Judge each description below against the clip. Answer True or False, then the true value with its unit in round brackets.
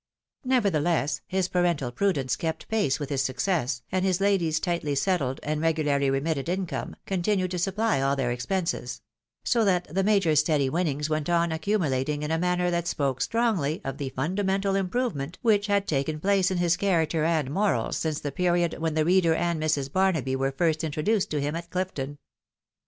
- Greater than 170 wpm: True (185 wpm)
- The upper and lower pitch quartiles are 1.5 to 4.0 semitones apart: False (4.5 semitones)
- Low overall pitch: False (165 Hz)